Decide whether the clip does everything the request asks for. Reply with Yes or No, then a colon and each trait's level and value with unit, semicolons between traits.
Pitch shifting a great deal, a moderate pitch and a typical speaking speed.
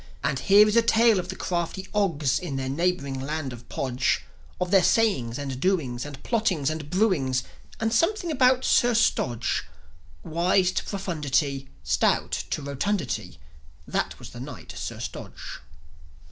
Yes: wide, 7.2 semitones; medium, 170 Hz; average, 150 wpm